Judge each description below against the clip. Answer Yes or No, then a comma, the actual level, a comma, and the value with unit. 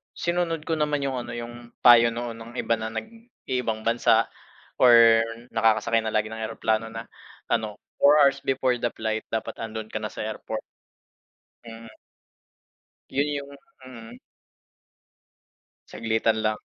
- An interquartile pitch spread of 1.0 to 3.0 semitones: Yes, narrow, 2.6 semitones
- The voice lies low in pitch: Yes, low, 115 Hz